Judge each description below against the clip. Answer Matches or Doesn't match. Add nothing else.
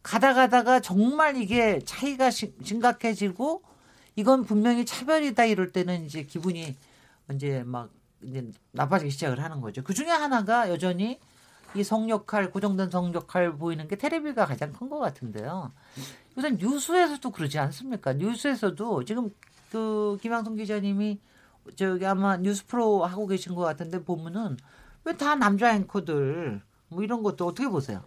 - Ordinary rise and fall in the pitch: Doesn't match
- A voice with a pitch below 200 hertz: Doesn't match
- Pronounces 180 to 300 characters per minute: Doesn't match